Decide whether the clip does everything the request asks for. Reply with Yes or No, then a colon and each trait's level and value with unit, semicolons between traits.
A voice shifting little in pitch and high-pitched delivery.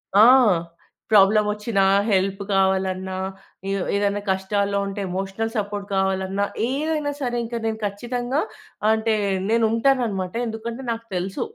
No: average, 3.0 semitones; high, 205 Hz